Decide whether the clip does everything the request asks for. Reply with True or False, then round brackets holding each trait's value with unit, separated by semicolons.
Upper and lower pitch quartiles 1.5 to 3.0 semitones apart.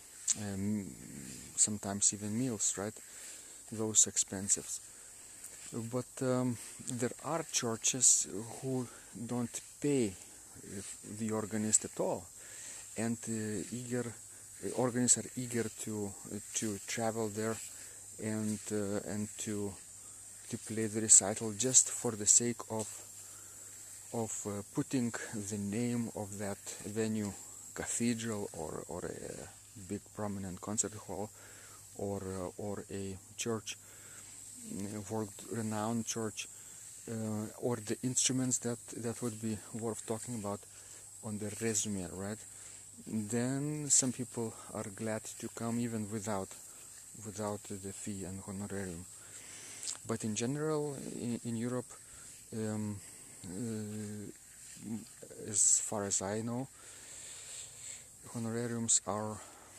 True (2.5 semitones)